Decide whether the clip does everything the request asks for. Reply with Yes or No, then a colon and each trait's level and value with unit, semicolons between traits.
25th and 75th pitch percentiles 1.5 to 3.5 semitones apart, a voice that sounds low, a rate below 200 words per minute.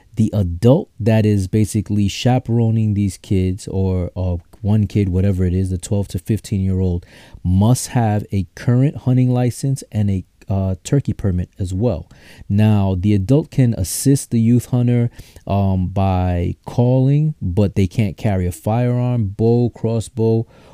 No: average, 4.0 semitones; low, 105 Hz; average, 155 wpm